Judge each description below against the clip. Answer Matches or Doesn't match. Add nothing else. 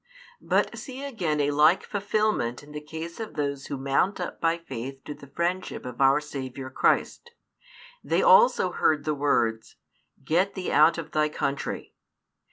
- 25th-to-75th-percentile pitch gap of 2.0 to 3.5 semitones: Doesn't match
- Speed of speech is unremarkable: Matches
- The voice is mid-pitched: Matches